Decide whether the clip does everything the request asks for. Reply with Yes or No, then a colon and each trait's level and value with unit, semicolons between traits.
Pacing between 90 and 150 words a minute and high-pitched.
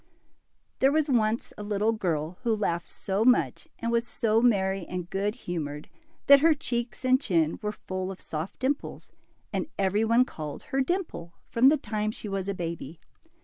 No: average, 185 wpm; high, 210 Hz